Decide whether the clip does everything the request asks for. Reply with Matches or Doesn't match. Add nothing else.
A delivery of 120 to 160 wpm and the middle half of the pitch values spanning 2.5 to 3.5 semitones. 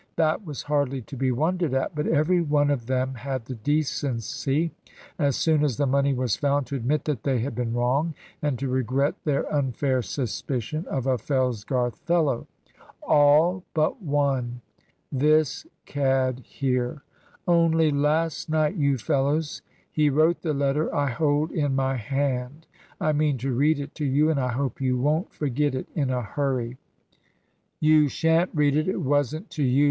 Doesn't match